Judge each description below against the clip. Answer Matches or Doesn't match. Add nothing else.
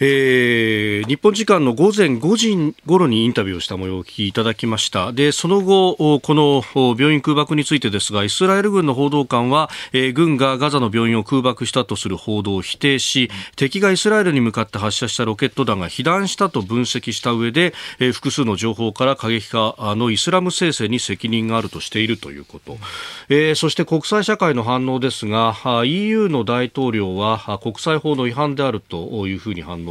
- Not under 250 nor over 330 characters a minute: Doesn't match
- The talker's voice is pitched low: Matches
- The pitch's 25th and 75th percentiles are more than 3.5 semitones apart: Matches